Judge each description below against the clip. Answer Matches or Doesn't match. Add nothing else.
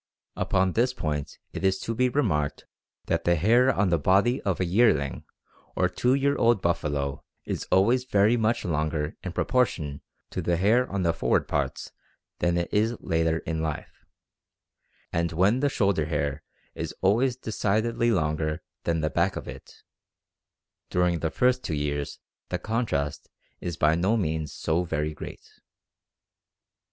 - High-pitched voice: Doesn't match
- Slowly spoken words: Doesn't match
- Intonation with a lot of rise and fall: Matches